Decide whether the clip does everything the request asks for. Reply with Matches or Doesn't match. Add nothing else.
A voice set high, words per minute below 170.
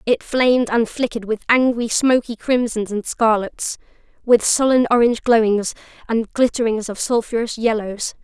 Matches